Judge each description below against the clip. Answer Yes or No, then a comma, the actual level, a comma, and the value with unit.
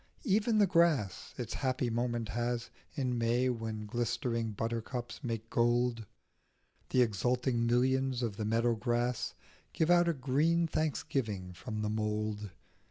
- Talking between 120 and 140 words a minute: Yes, slow, 135 wpm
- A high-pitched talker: No, low, 120 Hz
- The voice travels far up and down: No, average, 2.7 semitones